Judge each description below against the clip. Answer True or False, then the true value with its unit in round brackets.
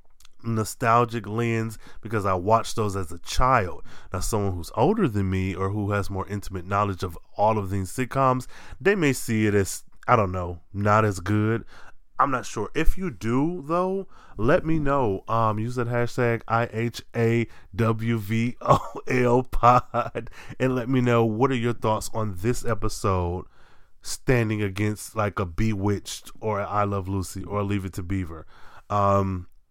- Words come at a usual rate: True (175 wpm)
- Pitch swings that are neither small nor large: True (3.3 semitones)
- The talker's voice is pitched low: True (110 Hz)